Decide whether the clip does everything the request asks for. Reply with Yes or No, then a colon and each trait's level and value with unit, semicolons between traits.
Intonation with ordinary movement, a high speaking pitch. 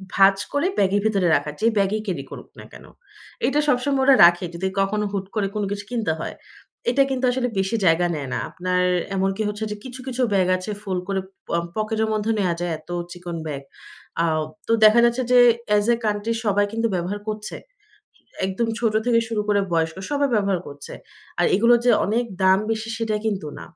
Yes: average, 3.4 semitones; high, 205 Hz